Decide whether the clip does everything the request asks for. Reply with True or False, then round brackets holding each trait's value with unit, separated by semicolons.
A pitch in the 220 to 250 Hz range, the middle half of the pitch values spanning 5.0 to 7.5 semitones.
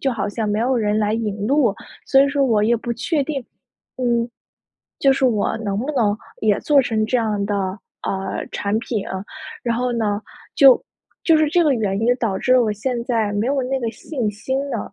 False (230 Hz; 3.9 semitones)